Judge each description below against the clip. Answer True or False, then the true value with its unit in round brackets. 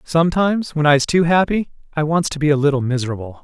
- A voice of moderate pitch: True (155 Hz)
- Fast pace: True (210 wpm)